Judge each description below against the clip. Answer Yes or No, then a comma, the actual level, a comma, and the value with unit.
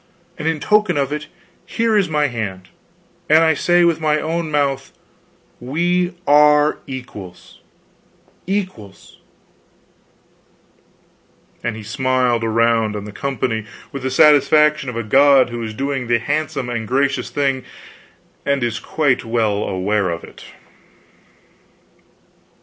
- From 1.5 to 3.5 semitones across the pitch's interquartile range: No, average, 4.8 semitones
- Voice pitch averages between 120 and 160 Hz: Yes, low, 135 Hz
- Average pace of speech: No, slow, 125 wpm